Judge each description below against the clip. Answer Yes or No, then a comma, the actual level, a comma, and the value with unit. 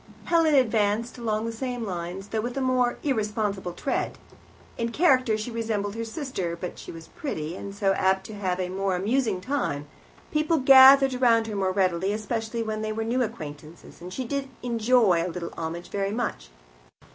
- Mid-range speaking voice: No, high, 215 Hz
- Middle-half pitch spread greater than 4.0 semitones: Yes, average, 4.7 semitones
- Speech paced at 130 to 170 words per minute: No, average, 180 wpm